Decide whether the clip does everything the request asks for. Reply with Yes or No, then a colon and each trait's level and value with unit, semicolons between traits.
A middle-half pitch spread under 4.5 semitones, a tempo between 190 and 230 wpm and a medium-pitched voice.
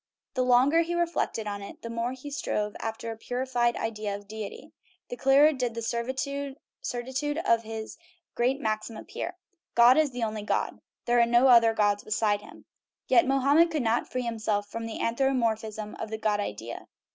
No: average, 3.3 semitones; average, 195 wpm; high, 235 Hz